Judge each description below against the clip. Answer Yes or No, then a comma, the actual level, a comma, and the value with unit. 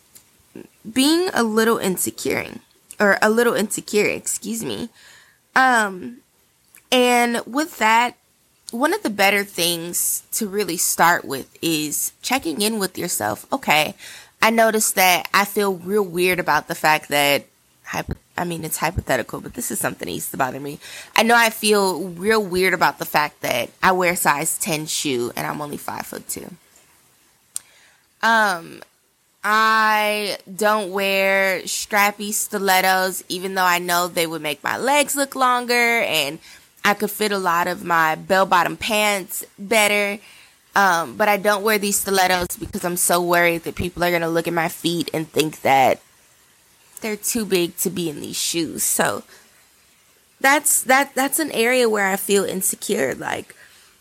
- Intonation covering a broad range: No, average, 4.1 semitones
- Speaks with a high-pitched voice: Yes, high, 200 Hz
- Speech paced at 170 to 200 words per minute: No, average, 160 wpm